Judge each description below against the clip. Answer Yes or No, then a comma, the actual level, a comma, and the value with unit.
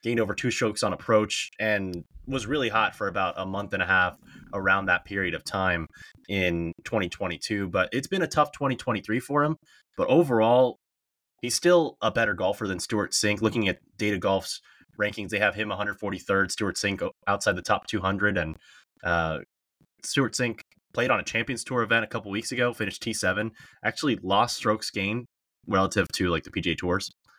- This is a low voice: Yes, low, 110 Hz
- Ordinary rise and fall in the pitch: Yes, average, 3.8 semitones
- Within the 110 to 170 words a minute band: No, average, 180 wpm